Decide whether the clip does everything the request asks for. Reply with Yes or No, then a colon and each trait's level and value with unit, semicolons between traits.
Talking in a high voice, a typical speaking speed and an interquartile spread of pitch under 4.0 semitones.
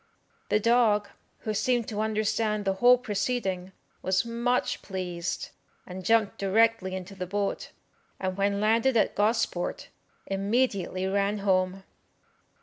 No: high, 205 Hz; slow, 125 wpm; average, 2.9 semitones